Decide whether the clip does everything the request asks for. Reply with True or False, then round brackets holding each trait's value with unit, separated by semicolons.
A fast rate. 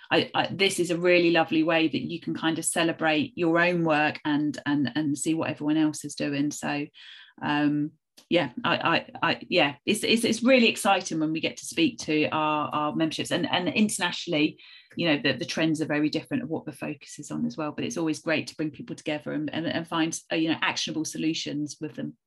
True (230 wpm)